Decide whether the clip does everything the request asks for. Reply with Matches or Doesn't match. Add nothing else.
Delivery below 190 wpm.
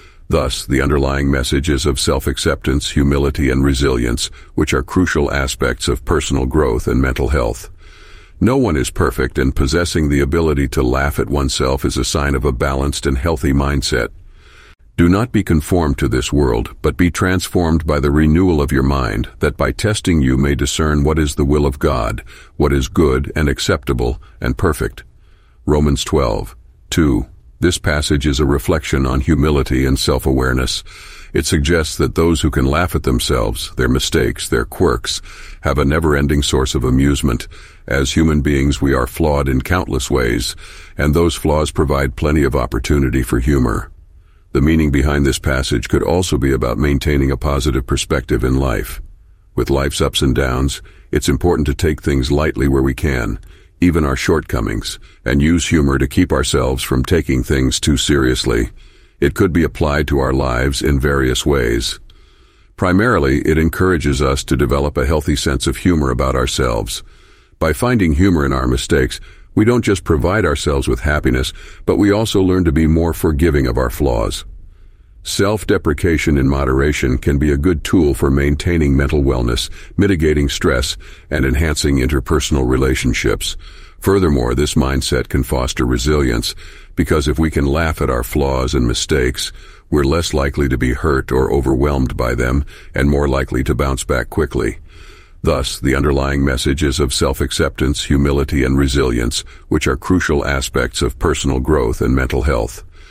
Matches